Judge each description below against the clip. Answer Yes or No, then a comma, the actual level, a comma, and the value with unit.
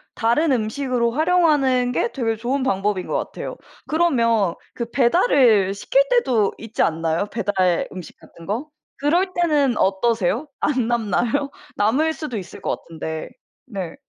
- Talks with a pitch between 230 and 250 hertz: Yes, high, 235 Hz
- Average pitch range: No, wide, 5.9 semitones